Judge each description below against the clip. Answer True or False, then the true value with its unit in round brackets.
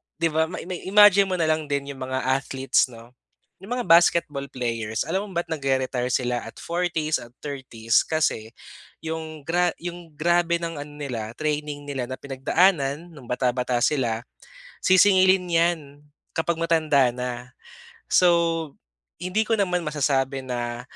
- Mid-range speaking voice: True (150 Hz)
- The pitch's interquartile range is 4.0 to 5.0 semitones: True (4.7 semitones)